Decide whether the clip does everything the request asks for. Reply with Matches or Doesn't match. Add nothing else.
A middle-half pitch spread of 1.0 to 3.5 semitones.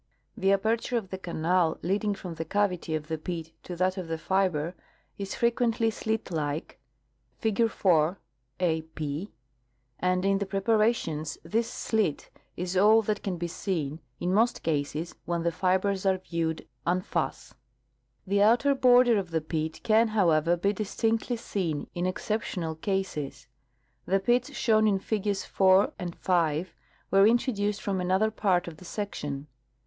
Doesn't match